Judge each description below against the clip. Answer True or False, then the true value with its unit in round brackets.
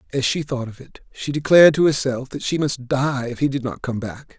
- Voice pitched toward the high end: False (135 Hz)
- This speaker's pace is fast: True (260 wpm)